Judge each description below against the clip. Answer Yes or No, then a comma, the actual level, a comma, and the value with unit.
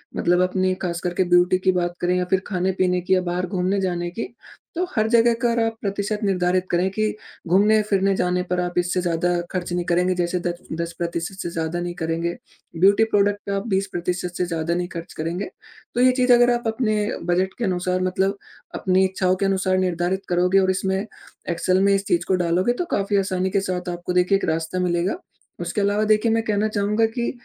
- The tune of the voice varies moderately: No, narrow, 2.2 semitones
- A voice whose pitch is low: No, medium, 185 Hz